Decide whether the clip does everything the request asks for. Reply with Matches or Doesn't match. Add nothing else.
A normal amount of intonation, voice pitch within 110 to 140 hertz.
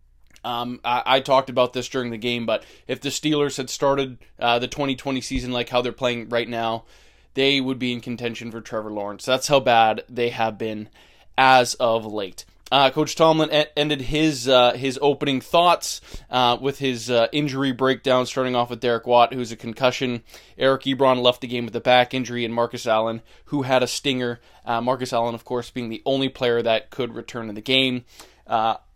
Doesn't match